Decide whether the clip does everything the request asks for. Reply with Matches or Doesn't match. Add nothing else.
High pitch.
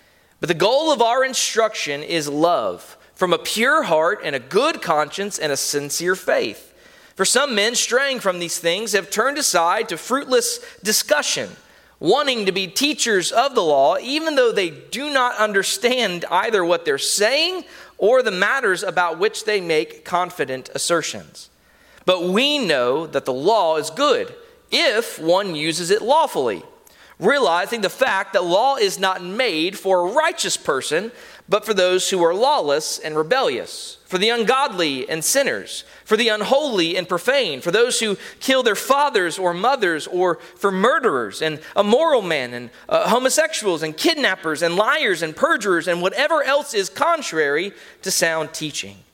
Matches